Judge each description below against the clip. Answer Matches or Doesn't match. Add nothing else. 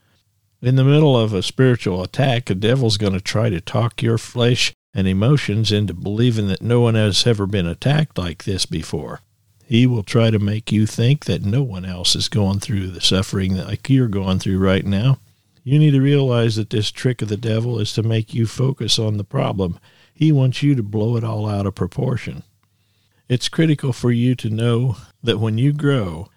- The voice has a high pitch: Doesn't match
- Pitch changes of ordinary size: Matches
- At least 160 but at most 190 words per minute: Doesn't match